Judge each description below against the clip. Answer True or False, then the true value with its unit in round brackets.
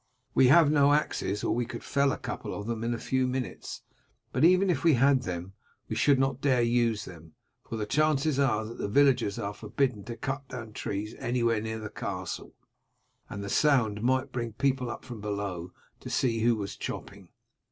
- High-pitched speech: False (120 Hz)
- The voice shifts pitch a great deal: False (4.4 semitones)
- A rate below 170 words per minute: False (200 wpm)